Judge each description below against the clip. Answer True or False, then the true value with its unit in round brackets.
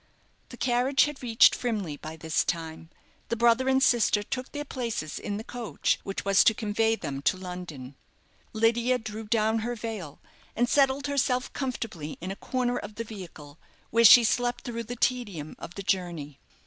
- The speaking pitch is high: True (225 Hz)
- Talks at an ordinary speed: True (175 wpm)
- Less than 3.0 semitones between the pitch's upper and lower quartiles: False (5.3 semitones)